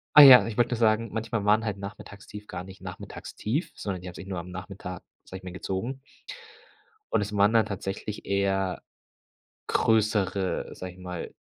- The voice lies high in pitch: No, low, 100 Hz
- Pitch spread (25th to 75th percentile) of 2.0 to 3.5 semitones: Yes, average, 2.8 semitones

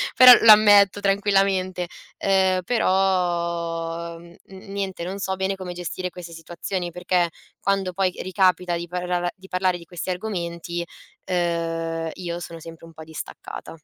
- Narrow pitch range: Yes, narrow, 2.0 semitones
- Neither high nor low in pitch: Yes, medium, 180 Hz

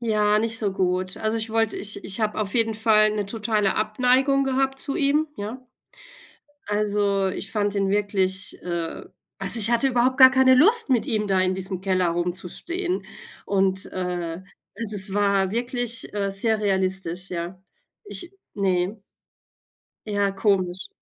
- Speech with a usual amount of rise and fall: Yes, average, 3.4 semitones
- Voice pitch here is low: No, high, 205 Hz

